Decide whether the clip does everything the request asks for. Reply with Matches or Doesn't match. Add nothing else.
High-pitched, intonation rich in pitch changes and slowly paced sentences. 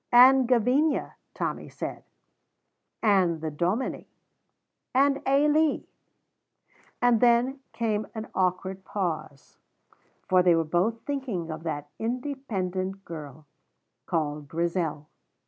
Matches